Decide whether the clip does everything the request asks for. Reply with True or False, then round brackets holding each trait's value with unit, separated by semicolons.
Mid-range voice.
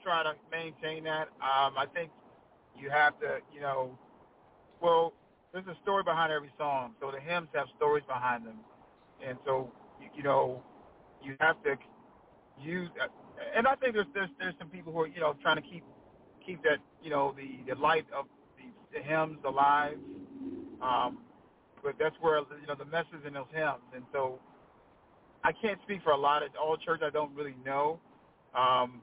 True (150 Hz)